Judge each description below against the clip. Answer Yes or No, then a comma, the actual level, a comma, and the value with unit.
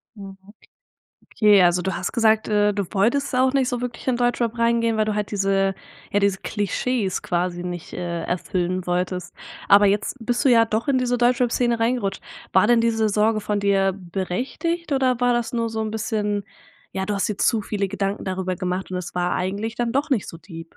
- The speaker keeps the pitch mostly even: No, average, 3.7 semitones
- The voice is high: Yes, high, 210 Hz